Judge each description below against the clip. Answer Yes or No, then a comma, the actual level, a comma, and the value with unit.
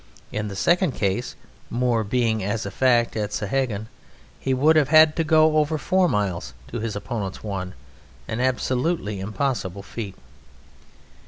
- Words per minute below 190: Yes, average, 150 wpm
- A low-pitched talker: Yes, low, 120 Hz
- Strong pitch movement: Yes, wide, 5.9 semitones